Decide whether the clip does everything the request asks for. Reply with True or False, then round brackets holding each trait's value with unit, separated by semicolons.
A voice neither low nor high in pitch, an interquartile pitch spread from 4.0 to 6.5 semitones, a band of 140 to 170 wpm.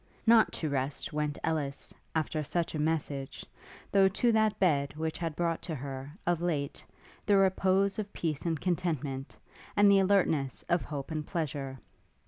True (160 Hz; 4.6 semitones; 160 wpm)